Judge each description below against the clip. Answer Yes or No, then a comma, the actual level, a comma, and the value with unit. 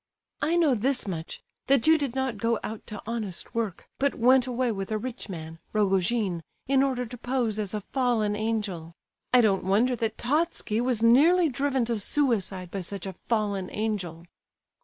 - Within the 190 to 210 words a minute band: No, average, 180 wpm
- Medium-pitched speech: No, high, 225 Hz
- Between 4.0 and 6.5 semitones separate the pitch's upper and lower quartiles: Yes, average, 4.3 semitones